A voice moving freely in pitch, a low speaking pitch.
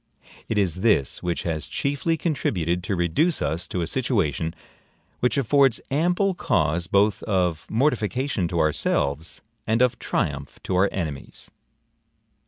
Yes: wide, 7.7 semitones; very low, 95 Hz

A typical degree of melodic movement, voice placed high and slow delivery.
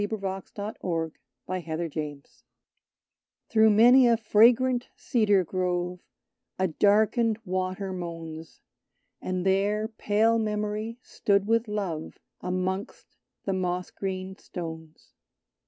Yes: average, 3.2 semitones; high, 195 Hz; slow, 105 wpm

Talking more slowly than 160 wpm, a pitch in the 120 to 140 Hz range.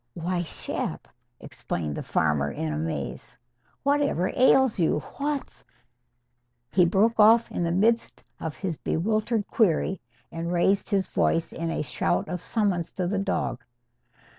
No: average, 140 wpm; medium, 180 Hz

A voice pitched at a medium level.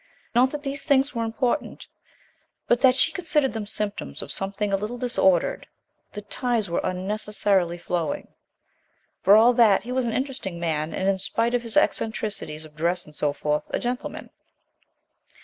No: high, 215 Hz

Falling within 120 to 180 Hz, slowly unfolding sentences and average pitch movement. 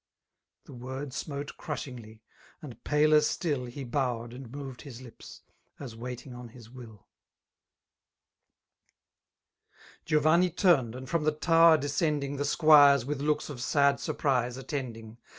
Yes: medium, 140 Hz; slow, 125 wpm; average, 3.4 semitones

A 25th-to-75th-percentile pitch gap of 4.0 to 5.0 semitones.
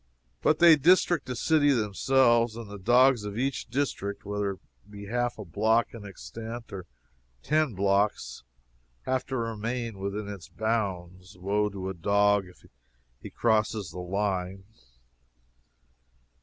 No: average, 3.5 semitones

